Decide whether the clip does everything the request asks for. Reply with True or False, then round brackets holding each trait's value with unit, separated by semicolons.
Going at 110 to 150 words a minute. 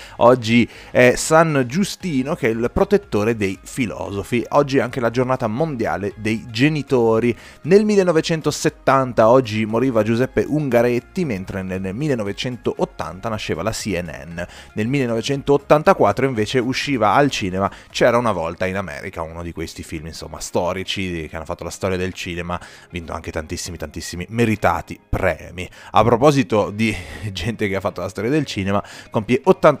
True (145 wpm)